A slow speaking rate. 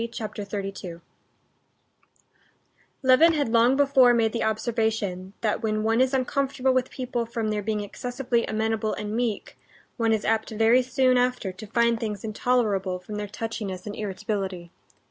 No: average, 150 wpm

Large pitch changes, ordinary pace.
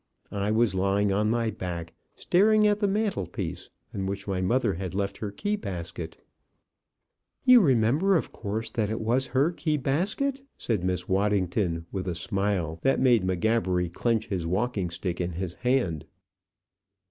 Yes: wide, 5.9 semitones; average, 160 wpm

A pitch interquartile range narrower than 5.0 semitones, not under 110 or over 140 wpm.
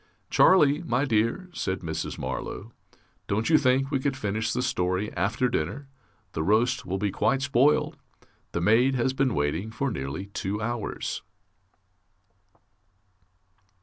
No: wide, 5.4 semitones; slow, 135 wpm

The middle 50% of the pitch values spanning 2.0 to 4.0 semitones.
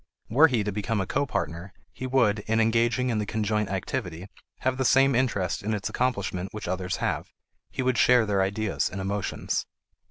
No: average, 4.5 semitones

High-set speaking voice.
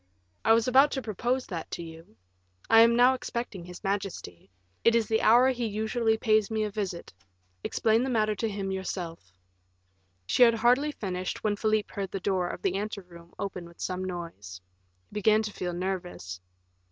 Yes: high, 205 Hz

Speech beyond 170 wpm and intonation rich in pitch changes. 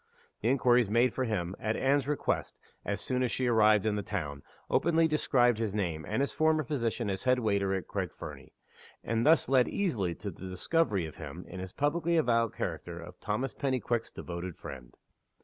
Yes: average, 190 wpm; wide, 5.7 semitones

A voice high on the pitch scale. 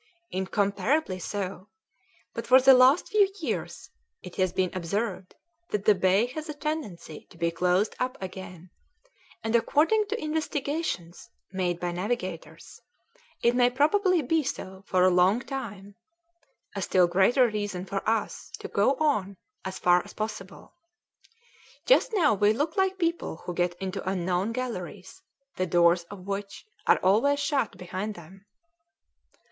Yes: high, 205 Hz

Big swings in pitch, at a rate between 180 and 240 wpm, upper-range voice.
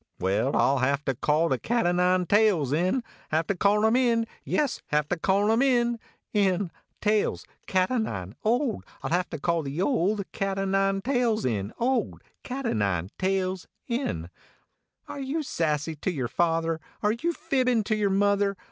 Yes: wide, 6.0 semitones; average, 185 wpm; high, 195 Hz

